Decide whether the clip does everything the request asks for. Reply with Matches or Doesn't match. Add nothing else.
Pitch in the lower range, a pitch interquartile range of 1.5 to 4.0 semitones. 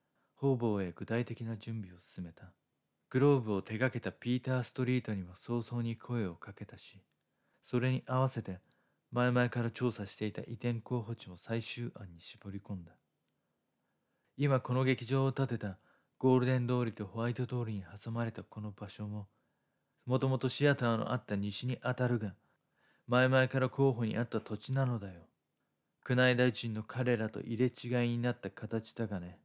Matches